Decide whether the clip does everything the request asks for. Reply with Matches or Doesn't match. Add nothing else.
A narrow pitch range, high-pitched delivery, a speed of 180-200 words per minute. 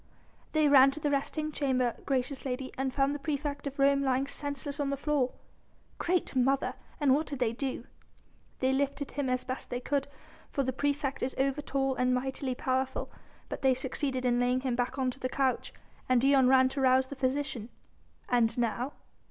Matches